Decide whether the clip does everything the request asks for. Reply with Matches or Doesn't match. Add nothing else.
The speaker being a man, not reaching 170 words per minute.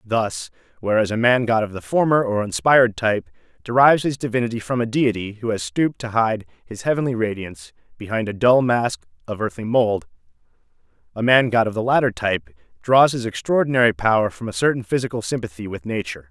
Doesn't match